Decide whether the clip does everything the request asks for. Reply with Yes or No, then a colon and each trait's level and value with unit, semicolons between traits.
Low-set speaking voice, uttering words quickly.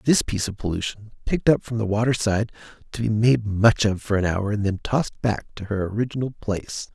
Yes: low, 110 Hz; fast, 225 wpm